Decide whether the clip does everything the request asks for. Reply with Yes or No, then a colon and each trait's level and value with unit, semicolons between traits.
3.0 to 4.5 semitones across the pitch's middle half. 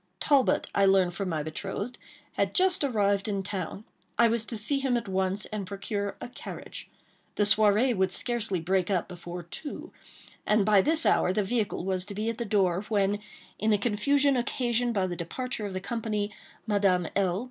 Yes: average, 3.5 semitones